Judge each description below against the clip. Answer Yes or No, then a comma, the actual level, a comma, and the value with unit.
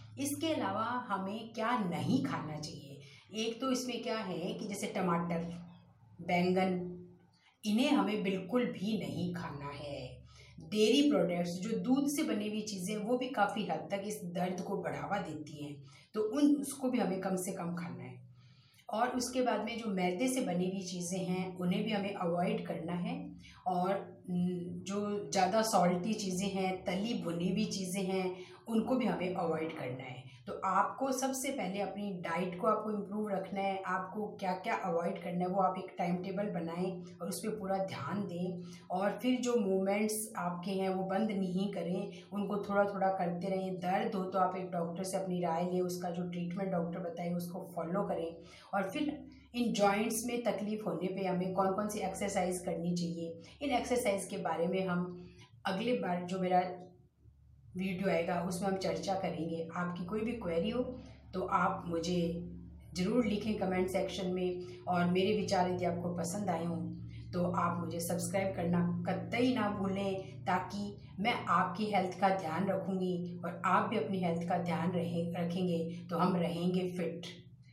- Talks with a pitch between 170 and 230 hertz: Yes, medium, 185 Hz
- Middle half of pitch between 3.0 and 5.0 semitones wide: No, narrow, 2.6 semitones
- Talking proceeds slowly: No, average, 175 wpm